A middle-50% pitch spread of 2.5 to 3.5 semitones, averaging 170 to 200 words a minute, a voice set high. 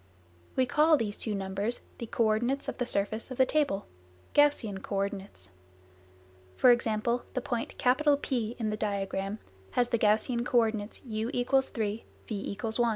No: average, 3.2 semitones; average, 160 wpm; high, 225 Hz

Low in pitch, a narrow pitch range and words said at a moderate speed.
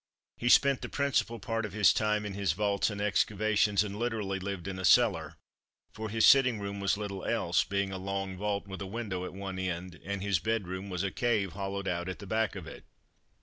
No: low, 100 Hz; narrow, 2.2 semitones; fast, 220 wpm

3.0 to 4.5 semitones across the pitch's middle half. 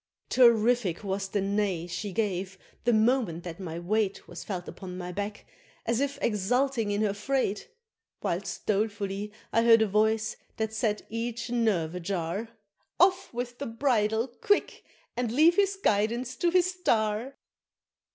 Yes: average, 3.6 semitones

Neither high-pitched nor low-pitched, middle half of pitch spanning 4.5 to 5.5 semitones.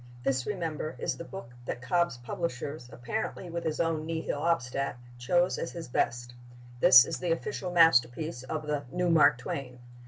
Yes: medium, 155 Hz; average, 5.1 semitones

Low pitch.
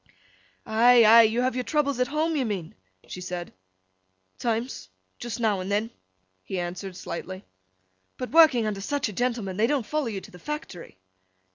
No: high, 225 Hz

